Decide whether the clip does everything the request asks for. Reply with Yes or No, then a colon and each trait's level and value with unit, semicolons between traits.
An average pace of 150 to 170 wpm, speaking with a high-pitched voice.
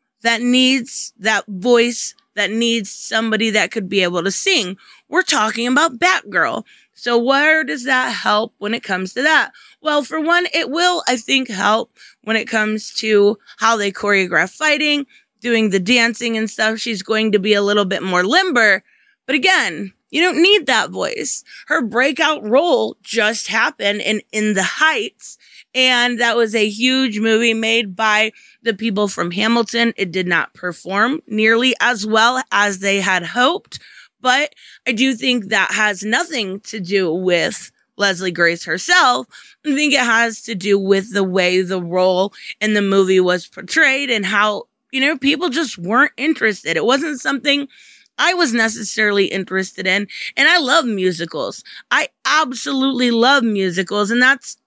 Yes: average, 165 wpm; high, 225 Hz